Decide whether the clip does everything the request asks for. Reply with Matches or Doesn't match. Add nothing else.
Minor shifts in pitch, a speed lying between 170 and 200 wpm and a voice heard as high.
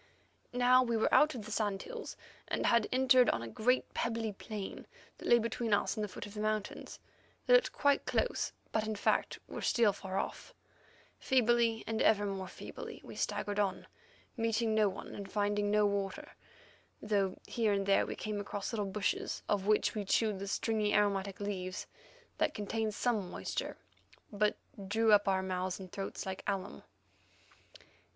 Matches